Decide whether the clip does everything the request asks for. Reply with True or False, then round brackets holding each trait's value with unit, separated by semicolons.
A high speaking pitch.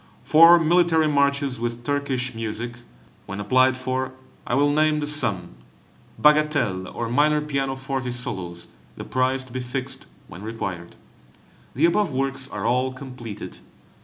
False (130 Hz)